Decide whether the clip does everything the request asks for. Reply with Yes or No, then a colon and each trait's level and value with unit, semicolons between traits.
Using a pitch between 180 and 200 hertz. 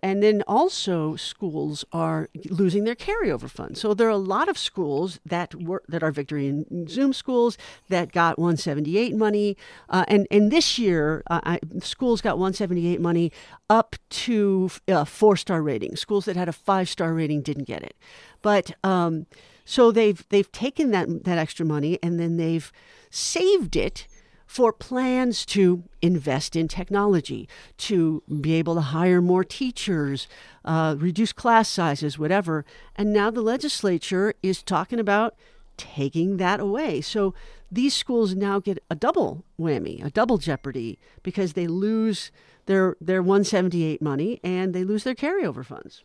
Yes: medium, 185 Hz